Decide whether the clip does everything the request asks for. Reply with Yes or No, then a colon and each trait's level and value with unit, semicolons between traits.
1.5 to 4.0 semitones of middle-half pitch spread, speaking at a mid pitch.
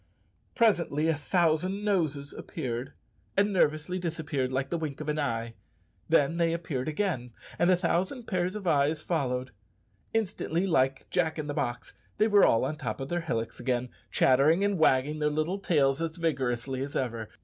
No: average, 4.6 semitones; medium, 155 Hz